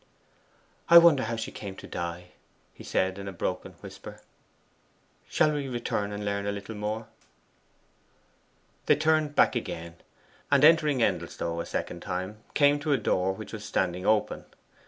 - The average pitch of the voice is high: No, low, 105 Hz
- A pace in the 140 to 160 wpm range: Yes, average, 155 wpm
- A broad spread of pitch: Yes, wide, 7.1 semitones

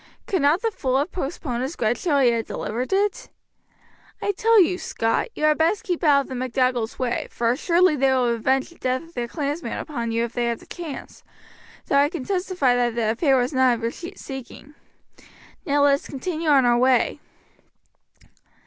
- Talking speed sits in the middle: Yes, average, 195 wpm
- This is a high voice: Yes, very high, 270 Hz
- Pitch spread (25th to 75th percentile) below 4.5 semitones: No, average, 5.2 semitones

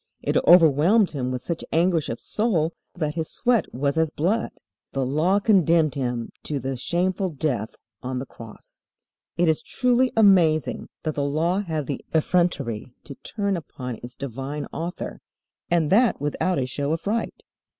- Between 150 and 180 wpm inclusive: Yes, average, 160 wpm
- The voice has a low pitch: No, medium, 160 Hz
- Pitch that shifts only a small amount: No, average, 4.9 semitones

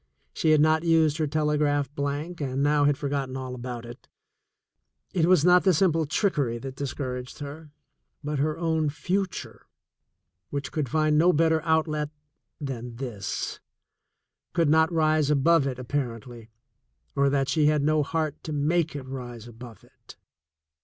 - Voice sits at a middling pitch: Yes, medium, 150 Hz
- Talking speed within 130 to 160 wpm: Yes, average, 155 wpm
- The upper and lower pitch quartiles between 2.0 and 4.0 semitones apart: Yes, average, 3.1 semitones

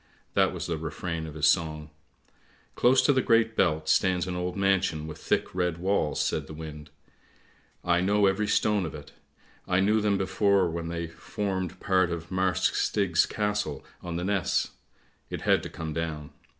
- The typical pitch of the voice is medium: No, very low, 90 Hz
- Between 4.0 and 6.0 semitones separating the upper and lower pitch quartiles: No, average, 3.5 semitones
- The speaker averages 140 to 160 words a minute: No, average, 190 wpm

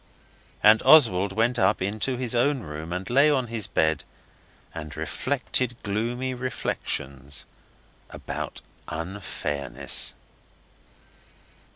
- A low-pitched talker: Yes, low, 105 Hz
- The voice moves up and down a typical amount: No, wide, 7.7 semitones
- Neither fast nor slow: No, slow, 95 wpm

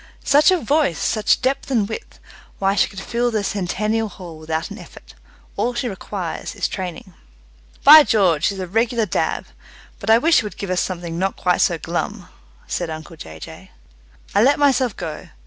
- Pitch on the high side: Yes, high, 200 Hz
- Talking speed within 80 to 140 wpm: No, average, 185 wpm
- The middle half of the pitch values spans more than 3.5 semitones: Yes, average, 5.2 semitones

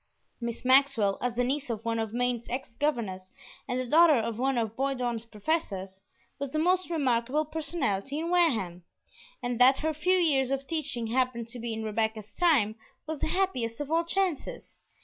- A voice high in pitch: Yes, very high, 255 Hz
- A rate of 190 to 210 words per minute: No, average, 180 wpm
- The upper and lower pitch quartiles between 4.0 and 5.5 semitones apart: Yes, average, 5.2 semitones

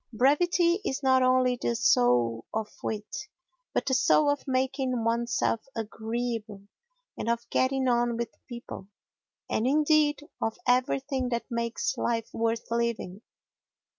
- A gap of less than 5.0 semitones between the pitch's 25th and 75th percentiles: Yes, average, 2.7 semitones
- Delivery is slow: Yes, slow, 130 wpm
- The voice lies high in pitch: Yes, high, 240 Hz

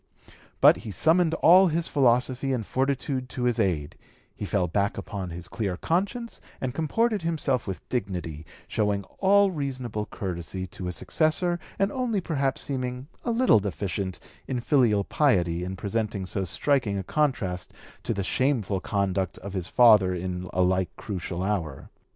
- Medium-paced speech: Yes, average, 155 wpm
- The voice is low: Yes, low, 110 Hz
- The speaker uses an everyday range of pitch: No, wide, 7.2 semitones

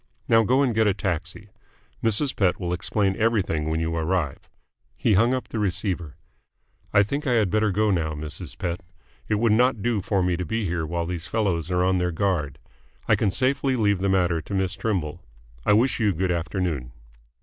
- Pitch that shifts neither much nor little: Yes, average, 4.1 semitones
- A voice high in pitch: No, very low, 95 Hz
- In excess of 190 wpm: Yes, average, 200 wpm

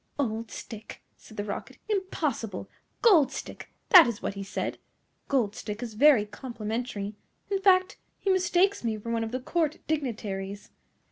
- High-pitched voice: Yes, high, 235 Hz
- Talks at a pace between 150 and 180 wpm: Yes, average, 155 wpm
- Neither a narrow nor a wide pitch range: No, wide, 7.4 semitones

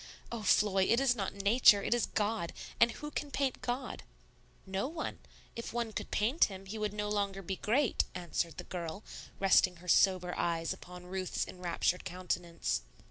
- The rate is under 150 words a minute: No, average, 175 wpm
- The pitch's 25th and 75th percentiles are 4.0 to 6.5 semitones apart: Yes, average, 4.4 semitones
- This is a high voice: Yes, high, 195 Hz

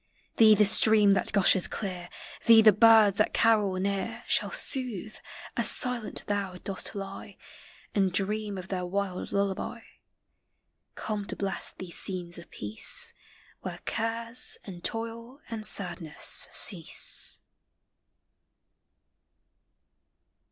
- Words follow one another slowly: Yes, slow, 115 wpm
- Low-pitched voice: No, high, 200 Hz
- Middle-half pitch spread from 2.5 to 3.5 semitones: Yes, average, 2.9 semitones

